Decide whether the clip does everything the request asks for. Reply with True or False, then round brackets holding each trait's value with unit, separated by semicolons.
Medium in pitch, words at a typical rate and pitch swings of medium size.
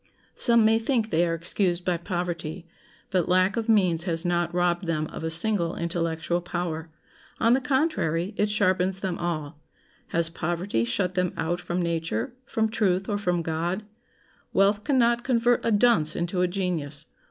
True (180 Hz; 170 wpm; 3.6 semitones)